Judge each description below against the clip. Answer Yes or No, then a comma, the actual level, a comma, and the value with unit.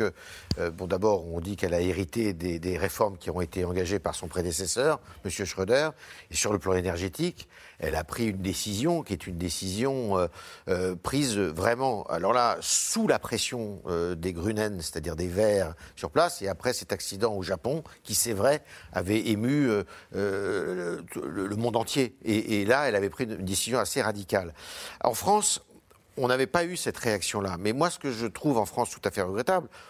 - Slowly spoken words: No, average, 200 wpm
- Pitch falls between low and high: No, low, 100 Hz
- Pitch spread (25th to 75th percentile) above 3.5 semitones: Yes, average, 4.4 semitones